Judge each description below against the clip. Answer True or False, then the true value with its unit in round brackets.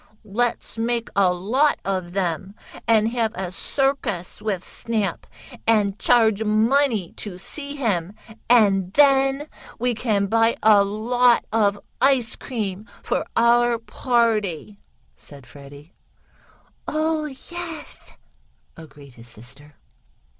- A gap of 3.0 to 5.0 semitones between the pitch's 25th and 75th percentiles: True (4.4 semitones)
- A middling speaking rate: False (110 wpm)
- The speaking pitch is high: True (220 Hz)